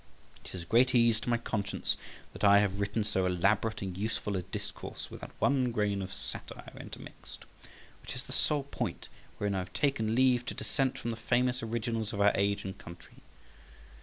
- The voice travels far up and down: No, average, 3.2 semitones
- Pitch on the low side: Yes, low, 110 Hz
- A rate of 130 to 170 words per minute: No, average, 190 wpm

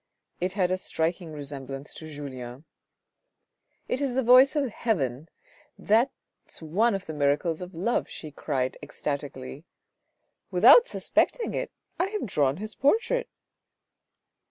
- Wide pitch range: Yes, wide, 8.8 semitones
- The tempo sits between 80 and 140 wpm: Yes, slow, 135 wpm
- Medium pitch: Yes, medium, 170 Hz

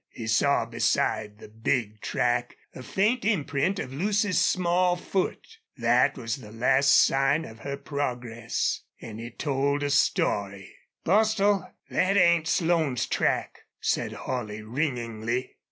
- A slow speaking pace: Yes, slow, 130 wpm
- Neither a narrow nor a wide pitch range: No, wide, 7.0 semitones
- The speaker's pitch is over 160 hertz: No, medium, 140 Hz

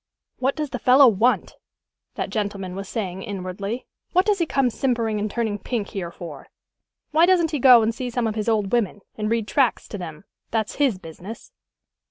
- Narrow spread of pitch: No, average, 4.3 semitones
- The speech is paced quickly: No, average, 195 wpm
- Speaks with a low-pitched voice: No, high, 225 Hz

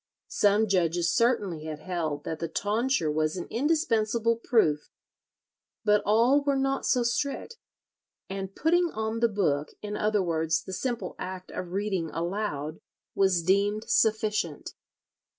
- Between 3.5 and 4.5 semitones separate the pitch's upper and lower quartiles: No, wide, 5.4 semitones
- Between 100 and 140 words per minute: Yes, slow, 135 wpm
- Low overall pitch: No, high, 205 Hz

